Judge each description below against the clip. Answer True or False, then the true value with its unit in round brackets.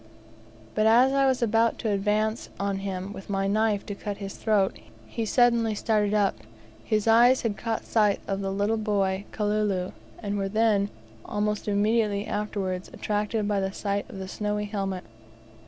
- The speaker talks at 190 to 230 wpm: False (170 wpm)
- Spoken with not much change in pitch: True (1.7 semitones)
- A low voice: False (210 Hz)